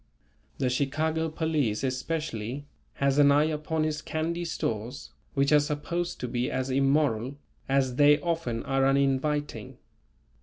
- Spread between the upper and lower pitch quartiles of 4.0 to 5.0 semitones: No, average, 2.9 semitones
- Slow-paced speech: Yes, slow, 130 wpm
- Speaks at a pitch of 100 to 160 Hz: Yes, medium, 140 Hz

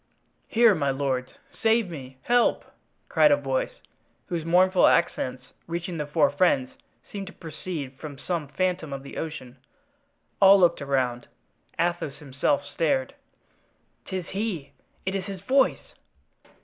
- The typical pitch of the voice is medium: Yes, medium, 165 Hz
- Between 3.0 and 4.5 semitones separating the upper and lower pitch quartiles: No, average, 5.3 semitones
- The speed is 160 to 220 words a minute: No, slow, 135 wpm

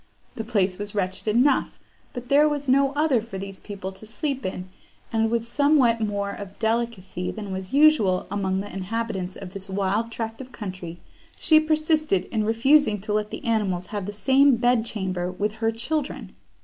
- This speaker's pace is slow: No, average, 180 wpm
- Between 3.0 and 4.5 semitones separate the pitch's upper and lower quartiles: No, average, 4.9 semitones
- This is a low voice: No, high, 220 Hz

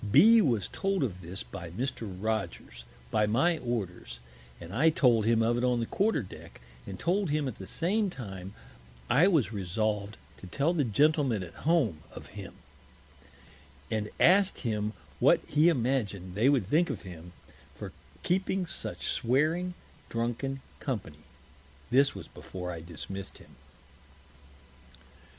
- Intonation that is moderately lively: No, wide, 7.8 semitones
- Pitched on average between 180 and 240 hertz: No, low, 115 Hz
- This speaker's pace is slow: No, average, 145 wpm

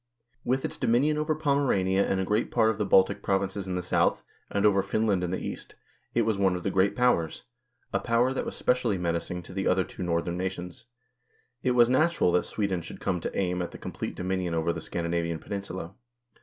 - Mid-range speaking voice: No, very low, 95 Hz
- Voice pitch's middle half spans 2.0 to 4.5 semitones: Yes, average, 3.9 semitones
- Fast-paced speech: Yes, fast, 210 wpm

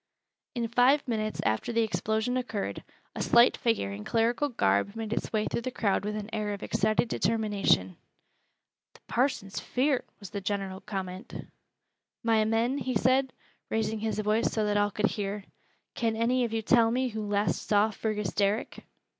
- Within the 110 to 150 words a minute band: No, average, 170 wpm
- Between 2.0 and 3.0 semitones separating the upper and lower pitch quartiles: Yes, narrow, 2.4 semitones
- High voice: Yes, high, 220 Hz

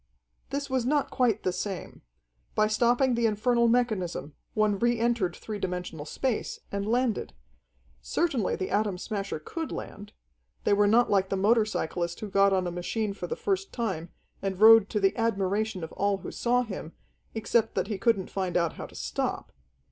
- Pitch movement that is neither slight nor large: Yes, average, 3.7 semitones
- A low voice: No, high, 210 Hz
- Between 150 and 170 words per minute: No, average, 180 wpm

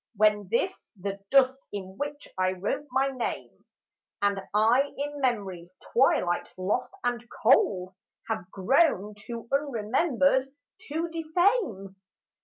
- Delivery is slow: Yes, slow, 115 wpm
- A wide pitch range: Yes, wide, 5.9 semitones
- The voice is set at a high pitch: Yes, high, 235 Hz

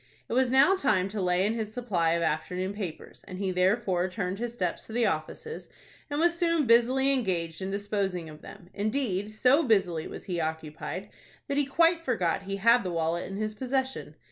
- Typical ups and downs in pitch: No, wide, 5.7 semitones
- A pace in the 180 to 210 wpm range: Yes, average, 195 wpm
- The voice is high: Yes, high, 205 Hz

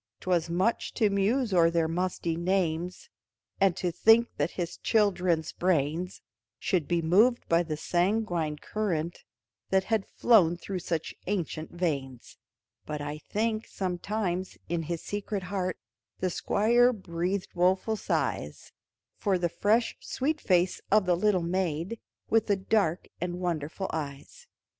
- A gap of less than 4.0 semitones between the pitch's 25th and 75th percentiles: Yes, average, 3.4 semitones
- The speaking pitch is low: No, medium, 180 Hz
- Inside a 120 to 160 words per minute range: Yes, average, 140 wpm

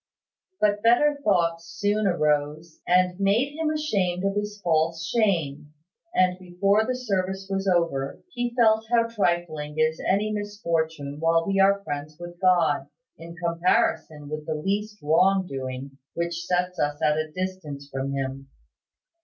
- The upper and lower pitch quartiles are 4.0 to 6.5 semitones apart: Yes, average, 4.6 semitones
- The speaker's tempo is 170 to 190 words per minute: No, average, 145 wpm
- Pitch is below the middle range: No, medium, 175 Hz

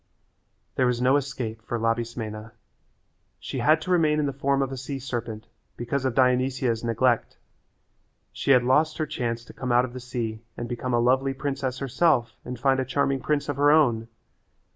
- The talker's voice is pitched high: No, low, 130 Hz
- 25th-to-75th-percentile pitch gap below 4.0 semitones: Yes, average, 2.7 semitones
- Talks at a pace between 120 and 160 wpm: No, average, 185 wpm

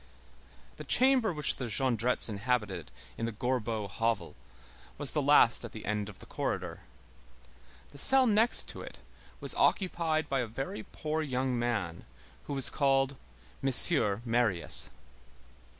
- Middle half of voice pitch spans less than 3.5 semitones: No, average, 5.0 semitones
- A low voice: Yes, low, 125 Hz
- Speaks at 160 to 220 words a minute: No, average, 140 wpm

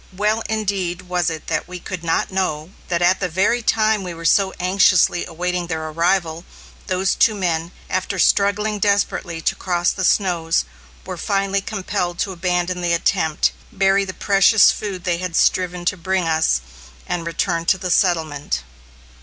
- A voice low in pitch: No, medium, 180 Hz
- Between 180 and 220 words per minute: No, average, 165 wpm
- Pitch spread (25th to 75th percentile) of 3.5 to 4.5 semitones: No, narrow, 2.4 semitones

